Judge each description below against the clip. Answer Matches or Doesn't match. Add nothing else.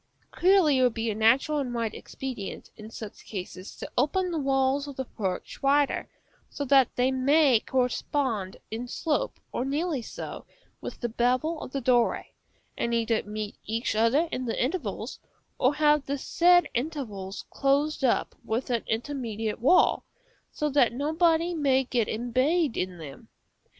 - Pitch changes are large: Doesn't match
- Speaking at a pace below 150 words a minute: Doesn't match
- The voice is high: Matches